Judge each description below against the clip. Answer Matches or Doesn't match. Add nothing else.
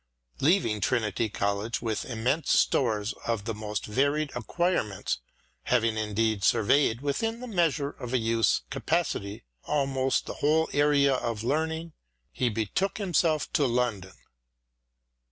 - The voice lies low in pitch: Matches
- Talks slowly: Matches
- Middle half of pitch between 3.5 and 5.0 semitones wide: Doesn't match